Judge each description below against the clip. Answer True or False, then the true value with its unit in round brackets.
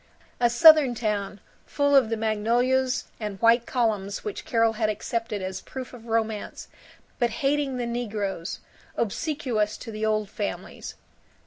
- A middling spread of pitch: True (3.0 semitones)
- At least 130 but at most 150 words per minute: True (140 wpm)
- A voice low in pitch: False (230 Hz)